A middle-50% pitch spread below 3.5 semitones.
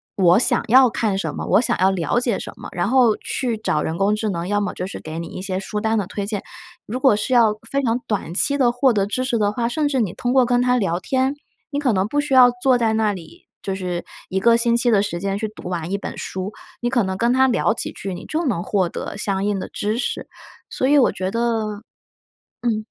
No: average, 4.1 semitones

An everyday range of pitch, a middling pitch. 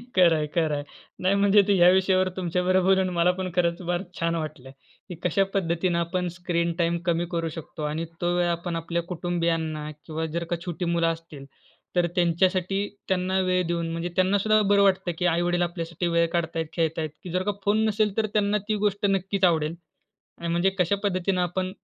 No: narrow, 1.9 semitones; medium, 175 Hz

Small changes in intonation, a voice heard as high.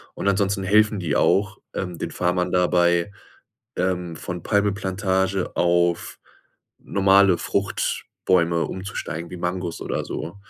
No: narrow, 2.0 semitones; very low, 95 Hz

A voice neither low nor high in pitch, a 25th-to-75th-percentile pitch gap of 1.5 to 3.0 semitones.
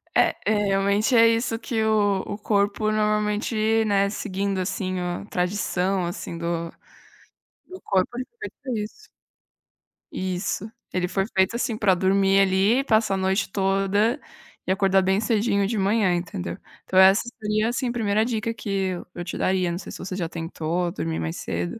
No: high, 195 Hz; average, 2.7 semitones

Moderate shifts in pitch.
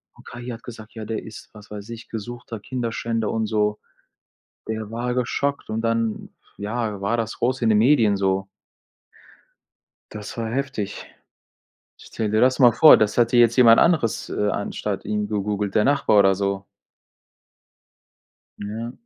No: narrow, 2.3 semitones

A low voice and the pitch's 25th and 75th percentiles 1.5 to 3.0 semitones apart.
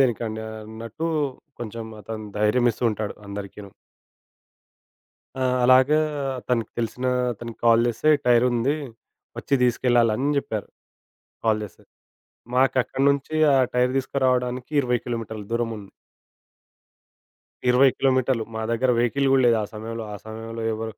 Yes: low, 120 Hz; narrow, 2.5 semitones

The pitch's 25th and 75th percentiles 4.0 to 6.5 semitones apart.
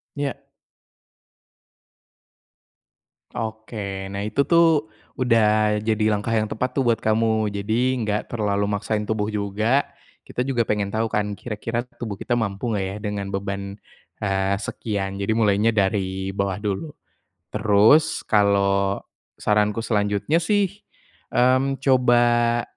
No: average, 2.8 semitones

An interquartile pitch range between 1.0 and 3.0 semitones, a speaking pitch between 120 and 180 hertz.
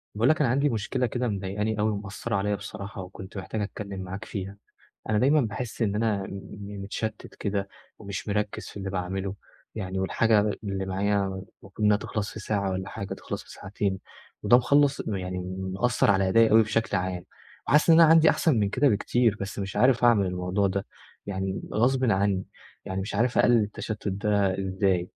No: average, 2.7 semitones; low, 105 Hz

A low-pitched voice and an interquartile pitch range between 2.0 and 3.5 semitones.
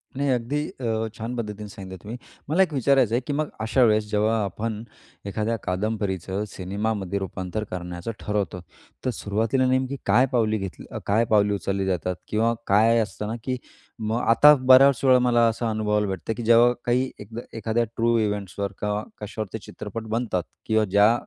Yes: low, 110 Hz; average, 2.8 semitones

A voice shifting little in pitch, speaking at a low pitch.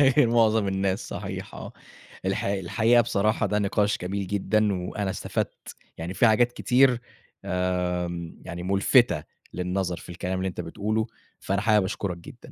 No: average, 3.2 semitones; low, 100 Hz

